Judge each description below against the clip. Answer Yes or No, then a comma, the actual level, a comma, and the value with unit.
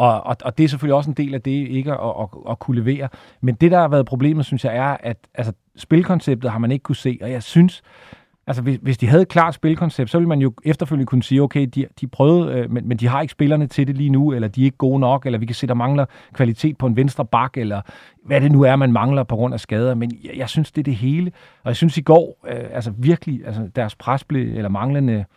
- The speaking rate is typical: No, fast, 270 wpm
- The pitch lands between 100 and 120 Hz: No, low, 135 Hz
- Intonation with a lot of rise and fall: No, average, 3.0 semitones